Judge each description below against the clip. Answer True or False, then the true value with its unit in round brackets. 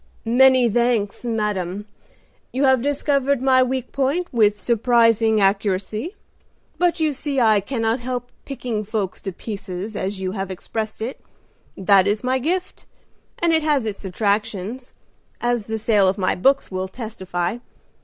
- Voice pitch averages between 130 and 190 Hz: False (225 Hz)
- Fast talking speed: False (145 wpm)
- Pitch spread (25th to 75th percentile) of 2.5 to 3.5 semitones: False (4.4 semitones)